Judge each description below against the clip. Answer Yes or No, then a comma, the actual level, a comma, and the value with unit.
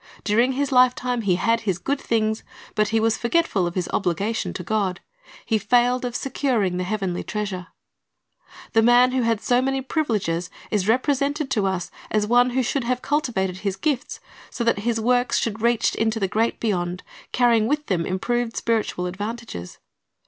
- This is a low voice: No, high, 225 Hz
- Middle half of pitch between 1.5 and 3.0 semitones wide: No, average, 4.1 semitones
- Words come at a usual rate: Yes, average, 180 wpm